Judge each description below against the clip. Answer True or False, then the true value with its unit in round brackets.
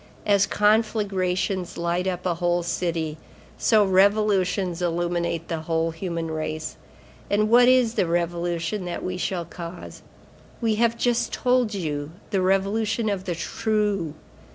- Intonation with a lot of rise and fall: False (3.7 semitones)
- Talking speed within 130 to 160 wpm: True (135 wpm)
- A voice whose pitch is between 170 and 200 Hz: True (185 Hz)